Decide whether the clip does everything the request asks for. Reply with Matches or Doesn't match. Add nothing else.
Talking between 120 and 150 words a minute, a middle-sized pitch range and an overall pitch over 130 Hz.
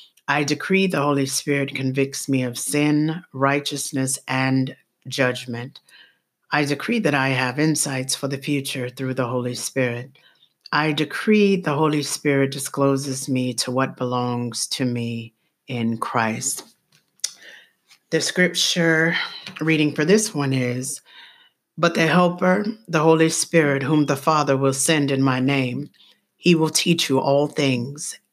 Matches